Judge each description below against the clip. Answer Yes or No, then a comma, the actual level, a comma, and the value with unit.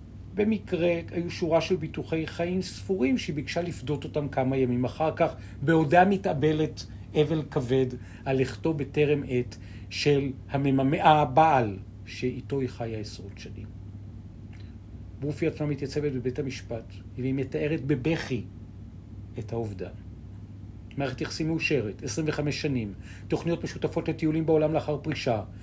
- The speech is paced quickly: No, average, 120 wpm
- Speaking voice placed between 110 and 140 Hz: Yes, low, 135 Hz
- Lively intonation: Yes, wide, 6.8 semitones